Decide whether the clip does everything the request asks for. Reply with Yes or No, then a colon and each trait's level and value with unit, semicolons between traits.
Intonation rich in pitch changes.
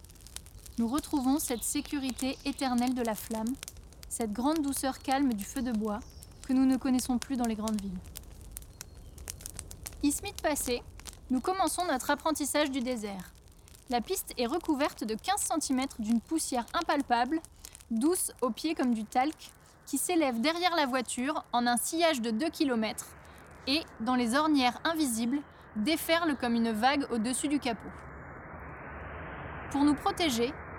No: average, 4.6 semitones